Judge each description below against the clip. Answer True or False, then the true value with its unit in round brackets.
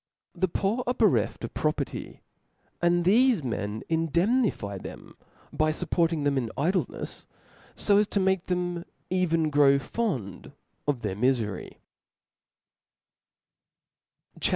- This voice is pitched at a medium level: True (165 Hz)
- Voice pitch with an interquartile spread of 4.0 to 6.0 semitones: True (5.6 semitones)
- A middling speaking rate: False (115 wpm)